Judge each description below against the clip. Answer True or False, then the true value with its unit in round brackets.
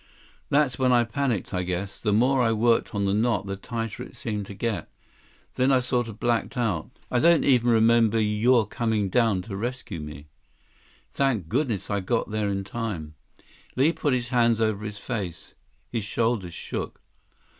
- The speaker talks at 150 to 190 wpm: True (175 wpm)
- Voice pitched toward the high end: False (115 Hz)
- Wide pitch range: False (3.3 semitones)